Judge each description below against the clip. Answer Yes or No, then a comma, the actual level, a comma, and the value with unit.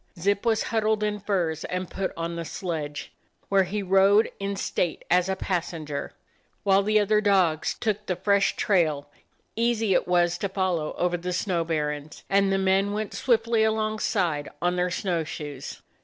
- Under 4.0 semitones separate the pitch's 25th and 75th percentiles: Yes, average, 3.3 semitones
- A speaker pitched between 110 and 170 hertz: No, high, 190 Hz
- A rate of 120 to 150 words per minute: No, average, 175 wpm